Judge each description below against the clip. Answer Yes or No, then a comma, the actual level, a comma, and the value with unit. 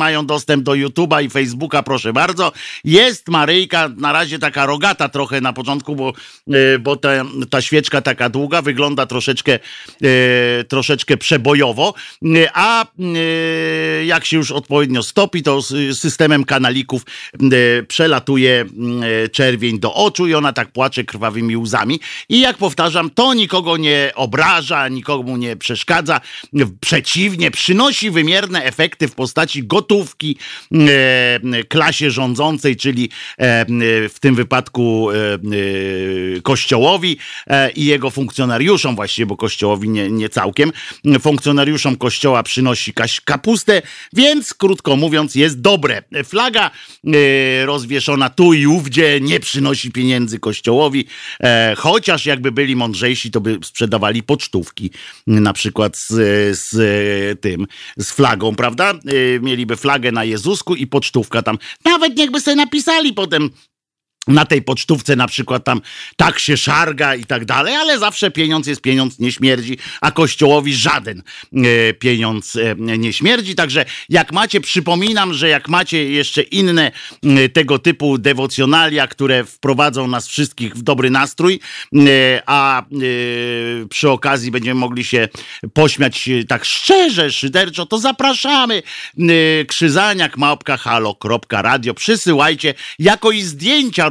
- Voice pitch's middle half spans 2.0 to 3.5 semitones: No, average, 4.6 semitones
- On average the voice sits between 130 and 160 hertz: Yes, medium, 140 Hz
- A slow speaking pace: No, average, 125 wpm